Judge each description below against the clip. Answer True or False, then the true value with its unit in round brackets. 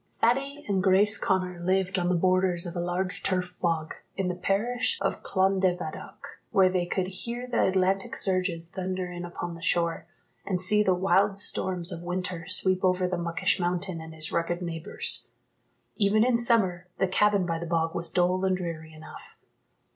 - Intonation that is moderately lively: False (1.8 semitones)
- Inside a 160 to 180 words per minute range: True (175 wpm)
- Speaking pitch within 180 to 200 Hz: True (185 Hz)